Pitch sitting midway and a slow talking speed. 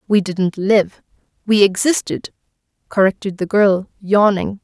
No: high, 195 Hz; slow, 105 wpm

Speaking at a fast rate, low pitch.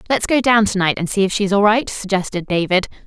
No: fast, 255 wpm; high, 200 Hz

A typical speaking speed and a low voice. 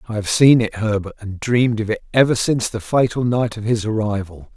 No: fast, 225 wpm; low, 110 Hz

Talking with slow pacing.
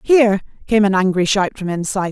No: average, 200 wpm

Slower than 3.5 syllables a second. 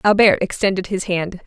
No: 5.3 syllables/s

